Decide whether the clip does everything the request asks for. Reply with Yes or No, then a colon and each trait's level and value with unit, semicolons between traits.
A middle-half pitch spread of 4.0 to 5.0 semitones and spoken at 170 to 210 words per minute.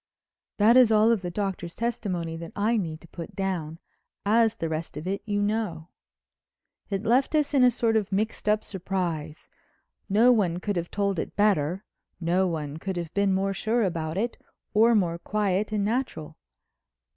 Yes: average, 4.3 semitones; average, 175 wpm